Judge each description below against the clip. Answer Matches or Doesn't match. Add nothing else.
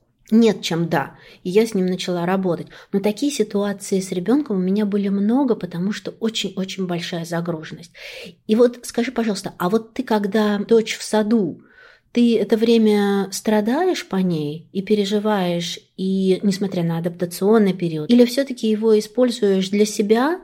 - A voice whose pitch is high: Matches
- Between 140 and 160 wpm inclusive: Matches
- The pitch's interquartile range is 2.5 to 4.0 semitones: Matches